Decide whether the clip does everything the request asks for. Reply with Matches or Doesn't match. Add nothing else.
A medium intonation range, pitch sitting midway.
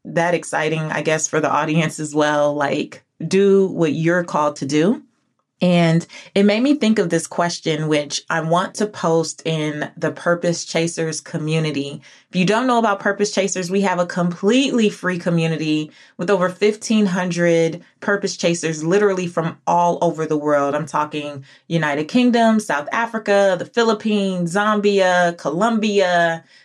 Matches